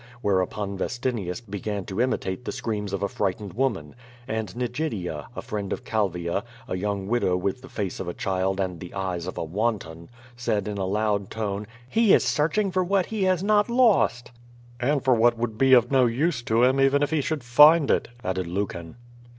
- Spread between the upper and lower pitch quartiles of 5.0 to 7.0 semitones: Yes, wide, 5.5 semitones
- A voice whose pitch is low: Yes, low, 110 Hz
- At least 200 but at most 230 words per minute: Yes, fast, 205 wpm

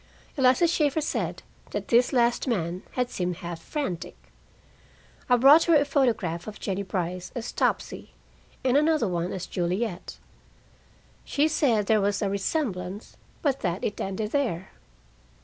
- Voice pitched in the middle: No, high, 220 Hz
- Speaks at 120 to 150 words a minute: Yes, average, 145 wpm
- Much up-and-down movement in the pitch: Yes, wide, 6.9 semitones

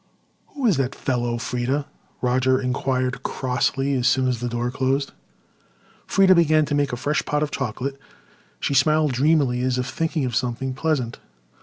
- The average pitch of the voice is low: Yes, low, 130 Hz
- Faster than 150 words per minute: Yes, average, 165 wpm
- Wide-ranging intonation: No, average, 2.7 semitones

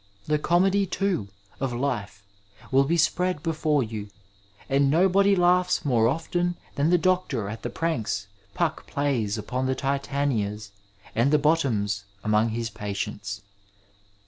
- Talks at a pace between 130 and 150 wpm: Yes, slow, 135 wpm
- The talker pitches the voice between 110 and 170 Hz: Yes, medium, 140 Hz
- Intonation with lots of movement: Yes, wide, 7.2 semitones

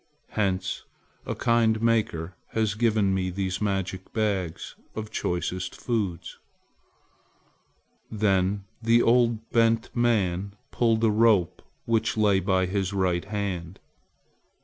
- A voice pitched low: Yes, low, 100 Hz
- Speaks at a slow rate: Yes, slow, 115 wpm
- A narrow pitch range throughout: No, average, 3.3 semitones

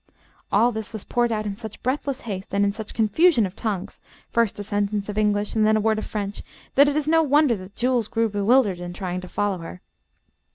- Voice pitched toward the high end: Yes, high, 215 Hz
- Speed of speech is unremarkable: No, fast, 235 wpm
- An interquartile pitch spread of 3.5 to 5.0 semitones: No, average, 2.9 semitones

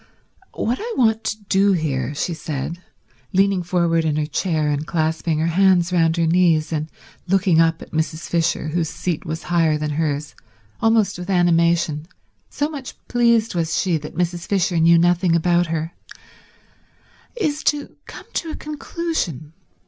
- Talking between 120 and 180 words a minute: Yes, average, 160 wpm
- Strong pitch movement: No, average, 3.4 semitones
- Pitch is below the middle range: No, medium, 170 Hz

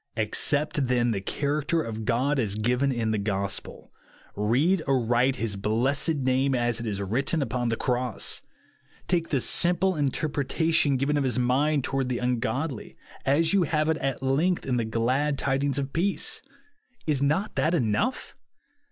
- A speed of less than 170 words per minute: Yes, average, 160 wpm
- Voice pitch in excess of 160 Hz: No, low, 135 Hz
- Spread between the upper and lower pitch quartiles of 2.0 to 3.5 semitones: No, average, 4.0 semitones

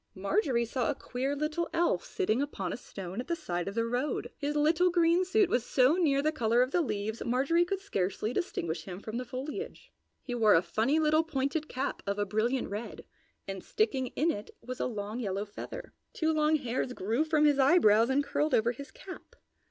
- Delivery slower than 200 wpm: No, fast, 205 wpm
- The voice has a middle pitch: No, very high, 260 Hz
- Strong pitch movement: Yes, wide, 6.1 semitones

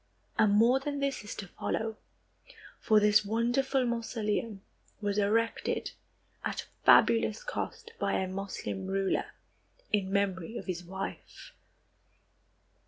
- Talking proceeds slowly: Yes, slow, 115 wpm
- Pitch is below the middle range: No, high, 210 Hz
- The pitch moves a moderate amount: Yes, average, 3.3 semitones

